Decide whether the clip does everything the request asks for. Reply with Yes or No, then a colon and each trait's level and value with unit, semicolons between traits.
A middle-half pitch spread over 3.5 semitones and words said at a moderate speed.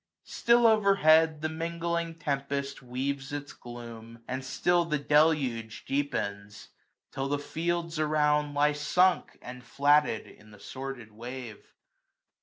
No: average, 4.3 semitones; slow, 125 wpm